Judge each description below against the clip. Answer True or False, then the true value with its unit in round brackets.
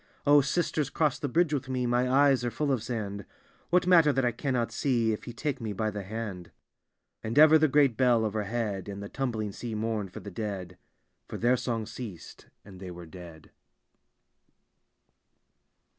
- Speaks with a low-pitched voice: True (115 Hz)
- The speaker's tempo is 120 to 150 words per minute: False (185 wpm)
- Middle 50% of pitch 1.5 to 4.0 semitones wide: False (4.6 semitones)